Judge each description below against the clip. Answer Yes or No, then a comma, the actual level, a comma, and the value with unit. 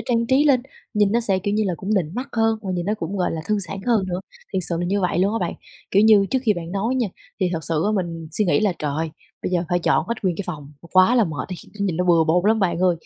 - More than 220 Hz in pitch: No, high, 190 Hz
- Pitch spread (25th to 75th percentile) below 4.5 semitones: Yes, average, 3.8 semitones